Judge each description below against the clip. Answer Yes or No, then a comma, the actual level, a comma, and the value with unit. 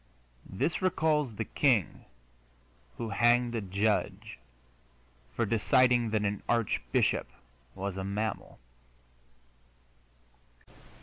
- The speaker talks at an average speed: No, slow, 85 wpm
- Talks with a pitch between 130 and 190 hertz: No, low, 110 Hz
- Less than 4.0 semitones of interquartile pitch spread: Yes, average, 3.5 semitones